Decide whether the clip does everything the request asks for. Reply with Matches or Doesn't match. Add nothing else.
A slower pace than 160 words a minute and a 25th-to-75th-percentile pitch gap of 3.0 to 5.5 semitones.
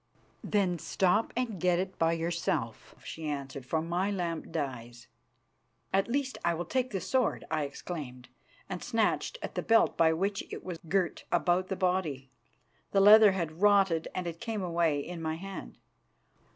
Doesn't match